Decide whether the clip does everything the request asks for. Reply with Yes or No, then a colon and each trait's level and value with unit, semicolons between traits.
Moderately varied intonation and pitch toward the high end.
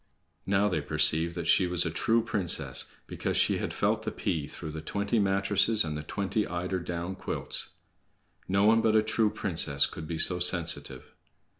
No: average, 3.8 semitones; very low, 90 Hz